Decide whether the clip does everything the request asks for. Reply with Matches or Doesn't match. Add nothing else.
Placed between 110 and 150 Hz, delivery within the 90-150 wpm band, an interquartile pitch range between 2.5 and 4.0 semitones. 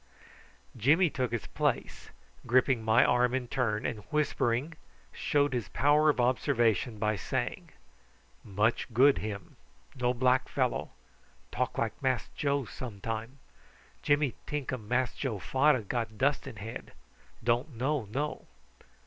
Matches